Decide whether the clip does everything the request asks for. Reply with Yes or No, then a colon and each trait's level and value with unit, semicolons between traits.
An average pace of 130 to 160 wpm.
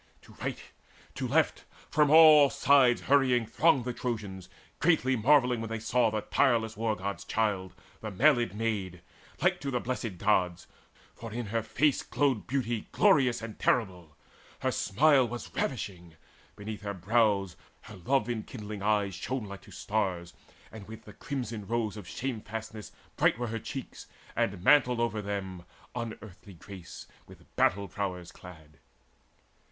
Yes: average, 150 wpm